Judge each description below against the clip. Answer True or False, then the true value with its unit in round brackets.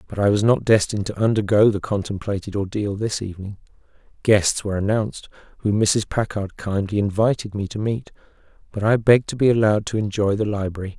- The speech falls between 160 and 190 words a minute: True (180 wpm)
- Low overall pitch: True (105 Hz)